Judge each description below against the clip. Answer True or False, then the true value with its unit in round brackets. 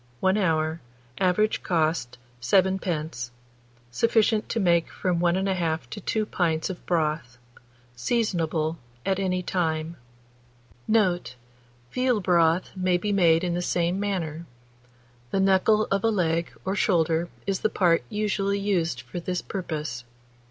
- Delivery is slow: True (130 wpm)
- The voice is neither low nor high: True (175 Hz)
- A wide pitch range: False (3.3 semitones)